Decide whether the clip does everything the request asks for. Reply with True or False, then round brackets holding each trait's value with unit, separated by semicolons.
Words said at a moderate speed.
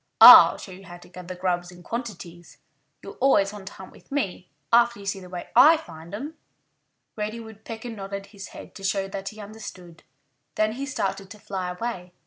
True (195 wpm)